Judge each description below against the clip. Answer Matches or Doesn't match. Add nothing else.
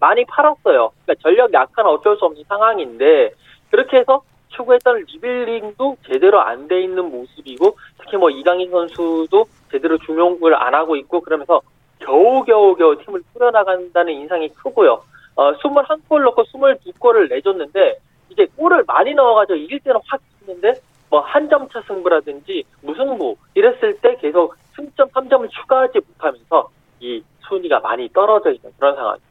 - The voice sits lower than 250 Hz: Doesn't match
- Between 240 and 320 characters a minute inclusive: Doesn't match